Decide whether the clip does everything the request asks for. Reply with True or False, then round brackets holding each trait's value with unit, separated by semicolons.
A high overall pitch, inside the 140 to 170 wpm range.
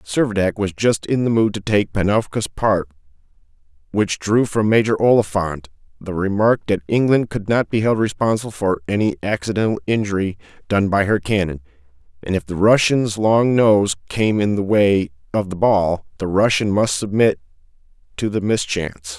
False (100 Hz; 165 wpm)